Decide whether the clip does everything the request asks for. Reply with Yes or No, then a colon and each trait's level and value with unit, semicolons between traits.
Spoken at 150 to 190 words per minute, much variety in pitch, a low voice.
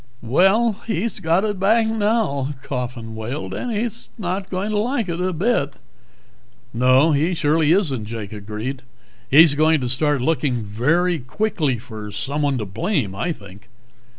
No: average, 155 wpm; wide, 7.7 semitones; medium, 150 Hz